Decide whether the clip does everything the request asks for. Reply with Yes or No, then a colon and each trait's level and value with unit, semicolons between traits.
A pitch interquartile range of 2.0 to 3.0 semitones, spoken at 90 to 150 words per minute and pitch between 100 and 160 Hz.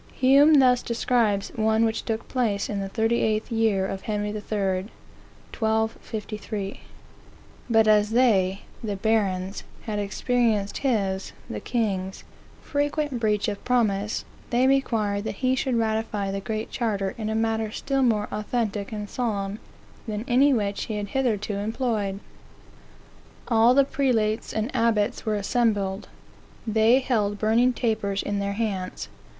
No: narrow, 2.6 semitones; average, 140 wpm; high, 220 Hz